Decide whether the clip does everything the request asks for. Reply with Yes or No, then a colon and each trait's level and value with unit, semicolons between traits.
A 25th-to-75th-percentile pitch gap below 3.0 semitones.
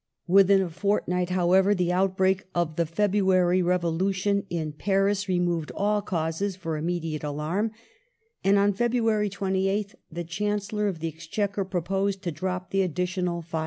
Yes: narrow, 2.5 semitones